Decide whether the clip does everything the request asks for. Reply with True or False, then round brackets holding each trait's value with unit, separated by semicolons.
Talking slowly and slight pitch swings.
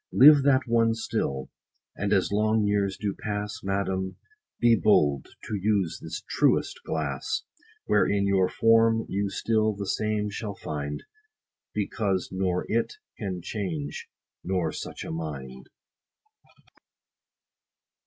False (120 wpm; 3.0 semitones)